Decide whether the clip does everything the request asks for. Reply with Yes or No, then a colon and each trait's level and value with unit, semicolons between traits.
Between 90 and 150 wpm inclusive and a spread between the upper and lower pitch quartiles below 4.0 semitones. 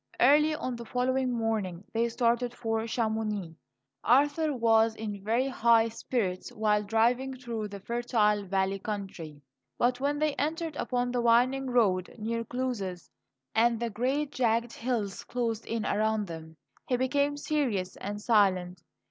Yes: average, 145 wpm; average, 3.2 semitones